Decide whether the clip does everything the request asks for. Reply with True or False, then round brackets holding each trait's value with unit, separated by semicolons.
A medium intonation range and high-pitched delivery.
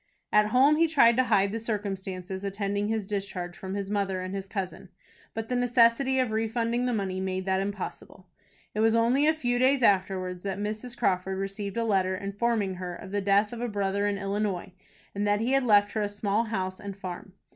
True (3.0 semitones; 205 Hz)